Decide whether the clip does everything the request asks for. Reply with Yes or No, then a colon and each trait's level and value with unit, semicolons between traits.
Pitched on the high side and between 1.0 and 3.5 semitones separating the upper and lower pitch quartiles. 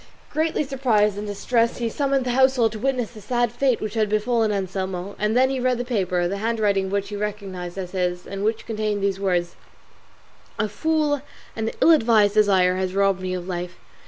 No: high, 210 Hz; average, 3.9 semitones